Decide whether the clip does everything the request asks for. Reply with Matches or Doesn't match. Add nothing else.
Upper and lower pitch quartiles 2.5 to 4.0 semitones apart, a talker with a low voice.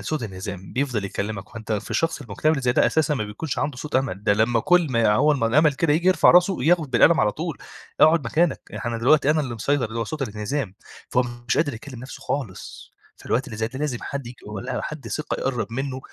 Doesn't match